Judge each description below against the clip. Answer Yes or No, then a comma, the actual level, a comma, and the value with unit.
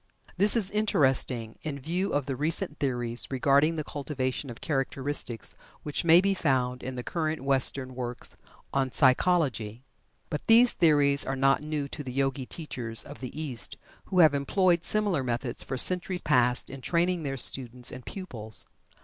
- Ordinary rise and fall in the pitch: Yes, average, 4.1 semitones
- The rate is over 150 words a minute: Yes, average, 165 wpm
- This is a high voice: No, medium, 140 Hz